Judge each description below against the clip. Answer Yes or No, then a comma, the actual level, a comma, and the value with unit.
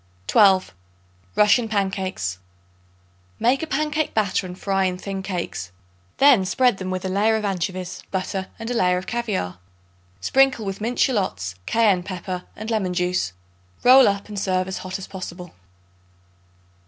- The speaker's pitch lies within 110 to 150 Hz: No, high, 195 Hz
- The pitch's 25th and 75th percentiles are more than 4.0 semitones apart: No, average, 3.1 semitones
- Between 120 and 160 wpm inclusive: Yes, average, 150 wpm